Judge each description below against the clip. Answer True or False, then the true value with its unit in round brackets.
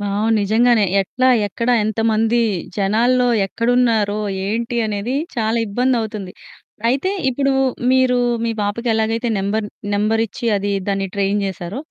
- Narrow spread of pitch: False (3.0 semitones)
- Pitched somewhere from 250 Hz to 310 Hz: False (220 Hz)